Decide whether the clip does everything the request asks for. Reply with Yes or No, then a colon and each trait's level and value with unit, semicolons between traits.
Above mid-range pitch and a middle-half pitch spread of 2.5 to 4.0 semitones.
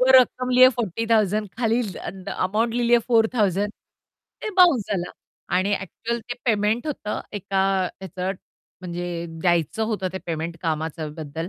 No: high, 205 Hz; average, 4.8 semitones